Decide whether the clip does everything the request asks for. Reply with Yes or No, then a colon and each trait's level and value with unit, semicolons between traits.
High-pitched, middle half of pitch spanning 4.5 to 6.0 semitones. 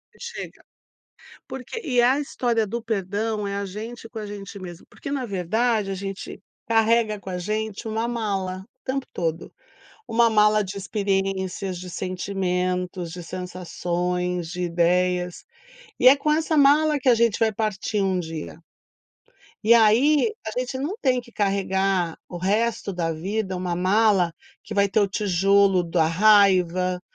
No: high, 200 Hz; average, 3.8 semitones